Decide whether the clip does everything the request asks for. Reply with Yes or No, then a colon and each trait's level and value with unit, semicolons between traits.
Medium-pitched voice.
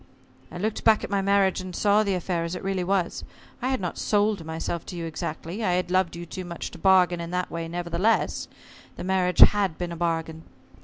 Yes: medium, 180 Hz